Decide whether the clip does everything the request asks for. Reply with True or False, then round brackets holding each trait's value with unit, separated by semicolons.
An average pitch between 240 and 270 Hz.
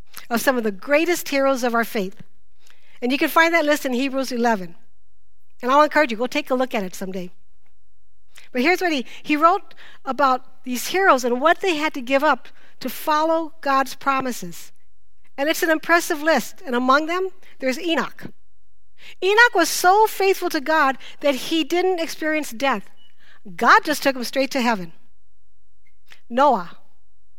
True (265 Hz)